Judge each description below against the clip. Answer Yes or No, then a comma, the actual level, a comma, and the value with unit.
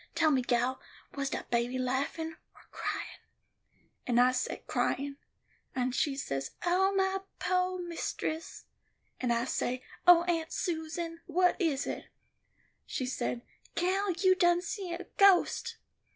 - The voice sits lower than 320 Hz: No, very high, 325 Hz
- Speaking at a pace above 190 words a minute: No, slow, 135 wpm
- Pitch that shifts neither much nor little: No, wide, 5.9 semitones